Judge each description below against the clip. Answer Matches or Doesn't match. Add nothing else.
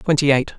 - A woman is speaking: Doesn't match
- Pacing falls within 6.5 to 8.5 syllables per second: Matches